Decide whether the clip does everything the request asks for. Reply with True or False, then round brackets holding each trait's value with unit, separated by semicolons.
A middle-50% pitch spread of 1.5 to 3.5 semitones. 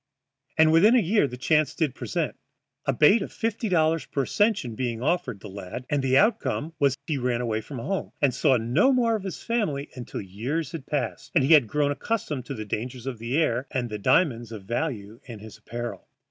False (5.6 semitones)